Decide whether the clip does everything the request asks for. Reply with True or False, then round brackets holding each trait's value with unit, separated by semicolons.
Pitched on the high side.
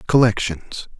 False (105 Hz)